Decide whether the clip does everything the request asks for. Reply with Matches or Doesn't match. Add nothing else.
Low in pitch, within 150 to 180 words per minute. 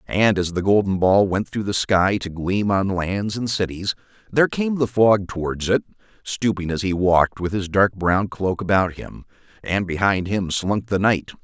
Doesn't match